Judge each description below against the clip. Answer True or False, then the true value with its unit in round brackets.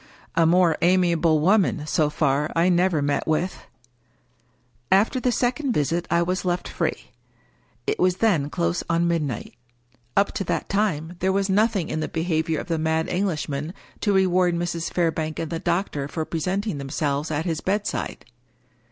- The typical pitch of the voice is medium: True (170 Hz)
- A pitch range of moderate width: True (3.2 semitones)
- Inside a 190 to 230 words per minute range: False (160 wpm)